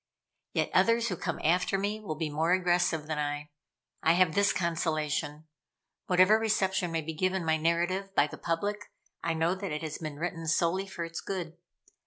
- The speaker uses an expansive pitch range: No, average, 3.0 semitones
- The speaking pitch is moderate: Yes, medium, 170 Hz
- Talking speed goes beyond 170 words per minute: Yes, average, 185 wpm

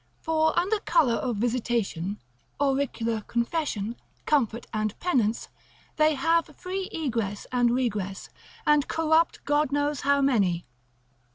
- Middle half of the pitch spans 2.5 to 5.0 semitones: No, wide, 5.4 semitones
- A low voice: No, very high, 265 Hz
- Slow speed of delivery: Yes, slow, 115 wpm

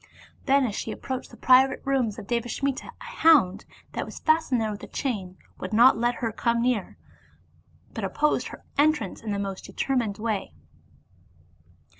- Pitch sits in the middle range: No, high, 240 Hz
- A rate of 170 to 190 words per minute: No, average, 160 wpm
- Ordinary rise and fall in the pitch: Yes, average, 4.3 semitones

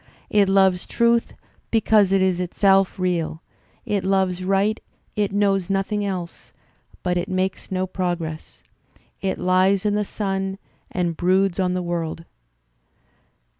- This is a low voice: No, high, 190 Hz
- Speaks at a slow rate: Yes, slow, 130 wpm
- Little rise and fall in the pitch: Yes, narrow, 1.5 semitones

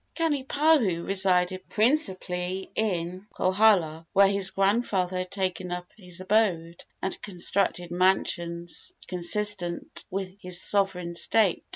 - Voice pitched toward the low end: No, medium, 185 Hz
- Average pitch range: No, narrow, 2.3 semitones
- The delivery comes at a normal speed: No, slow, 105 wpm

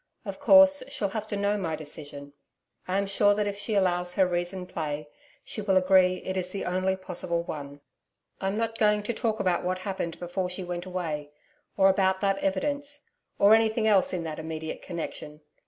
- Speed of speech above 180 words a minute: Yes, average, 190 wpm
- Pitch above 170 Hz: Yes, high, 190 Hz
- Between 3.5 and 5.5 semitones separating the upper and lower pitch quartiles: No, average, 2.8 semitones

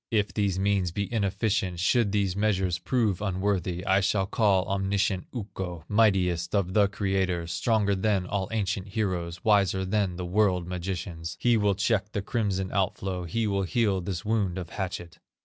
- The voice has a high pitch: No, very low, 95 Hz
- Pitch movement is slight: Yes, narrow, 2.2 semitones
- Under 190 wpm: Yes, average, 165 wpm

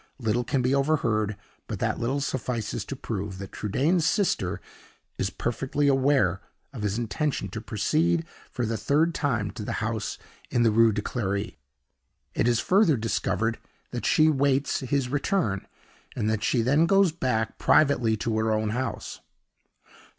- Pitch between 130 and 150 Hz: No, low, 120 Hz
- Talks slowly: No, average, 160 wpm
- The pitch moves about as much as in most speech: Yes, average, 4.7 semitones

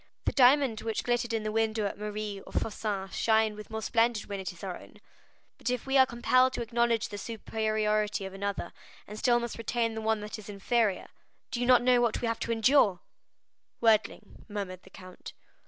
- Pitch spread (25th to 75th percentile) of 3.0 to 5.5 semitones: No, narrow, 2.4 semitones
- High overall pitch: Yes, high, 220 Hz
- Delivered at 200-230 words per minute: Yes, fast, 205 wpm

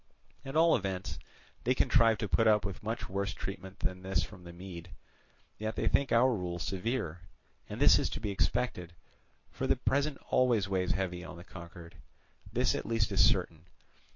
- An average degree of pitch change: Yes, average, 4.2 semitones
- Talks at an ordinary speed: Yes, average, 180 wpm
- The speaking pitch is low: Yes, very low, 95 Hz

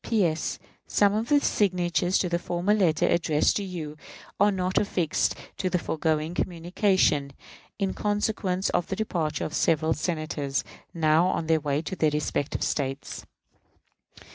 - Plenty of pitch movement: No, average, 3.5 semitones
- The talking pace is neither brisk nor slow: Yes, average, 145 wpm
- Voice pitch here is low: No, medium, 175 Hz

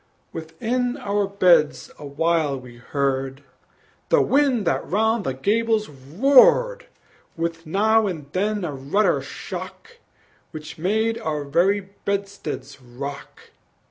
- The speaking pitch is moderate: Yes, medium, 180 Hz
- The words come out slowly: Yes, slow, 110 wpm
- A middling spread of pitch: No, wide, 7.2 semitones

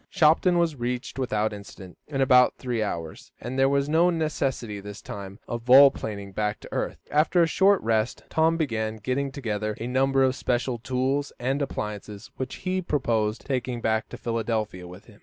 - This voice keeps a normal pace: Yes, average, 180 wpm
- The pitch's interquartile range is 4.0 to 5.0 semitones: Yes, average, 4.5 semitones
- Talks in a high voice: No, low, 125 Hz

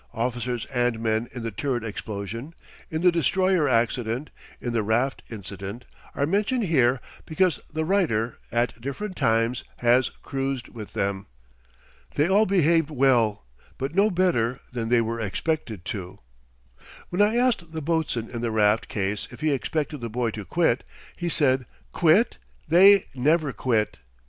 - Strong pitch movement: Yes, wide, 6.1 semitones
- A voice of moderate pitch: No, low, 125 Hz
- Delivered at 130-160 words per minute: Yes, average, 155 wpm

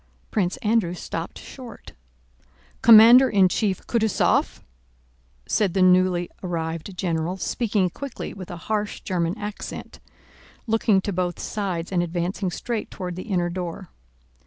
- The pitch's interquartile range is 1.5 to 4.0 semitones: Yes, average, 3.4 semitones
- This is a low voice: No, medium, 185 Hz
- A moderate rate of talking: No, slow, 130 wpm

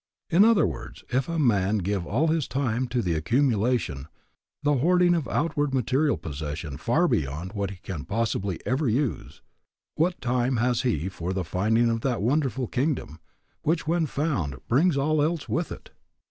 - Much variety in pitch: Yes, wide, 7.4 semitones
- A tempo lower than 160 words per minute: No, average, 170 wpm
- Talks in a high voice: No, low, 125 Hz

